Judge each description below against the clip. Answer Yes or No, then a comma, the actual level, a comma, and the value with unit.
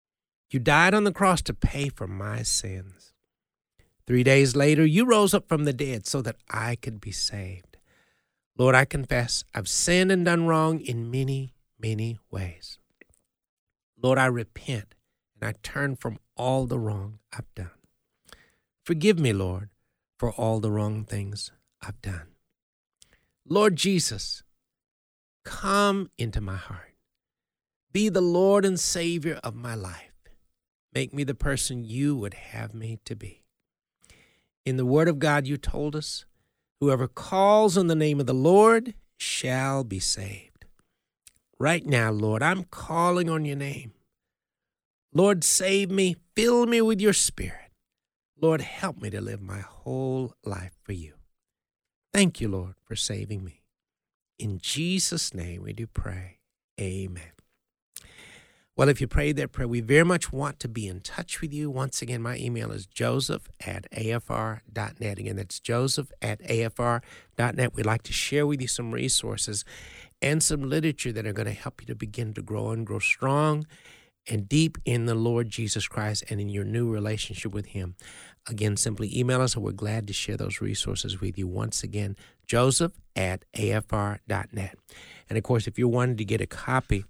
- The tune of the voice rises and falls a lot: Yes, wide, 5.8 semitones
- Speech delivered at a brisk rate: No, average, 165 wpm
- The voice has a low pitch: Yes, low, 120 Hz